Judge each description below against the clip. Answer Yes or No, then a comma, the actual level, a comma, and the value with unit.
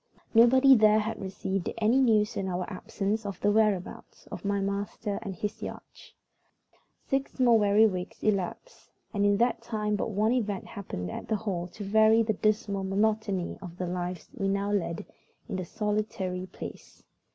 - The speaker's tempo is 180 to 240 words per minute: No, average, 170 wpm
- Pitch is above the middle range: Yes, high, 205 Hz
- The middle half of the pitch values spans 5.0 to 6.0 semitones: No, narrow, 2.4 semitones